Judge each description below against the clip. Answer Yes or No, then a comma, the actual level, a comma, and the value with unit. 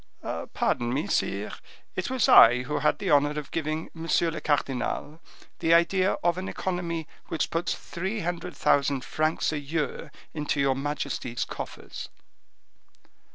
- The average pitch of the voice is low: No, medium, 155 Hz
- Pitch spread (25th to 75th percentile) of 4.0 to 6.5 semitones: No, average, 3.2 semitones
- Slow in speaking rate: No, average, 145 wpm